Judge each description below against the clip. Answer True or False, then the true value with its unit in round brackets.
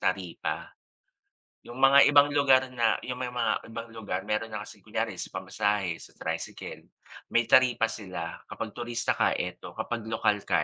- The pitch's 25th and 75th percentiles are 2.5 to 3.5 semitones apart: True (3.0 semitones)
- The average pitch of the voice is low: True (115 Hz)